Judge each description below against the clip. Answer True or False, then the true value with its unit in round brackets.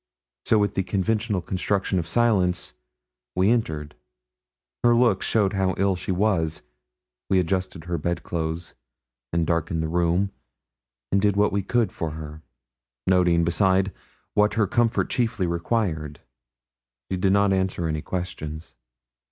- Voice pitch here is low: True (95 Hz)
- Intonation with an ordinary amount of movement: True (3.3 semitones)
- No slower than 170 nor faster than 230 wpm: False (140 wpm)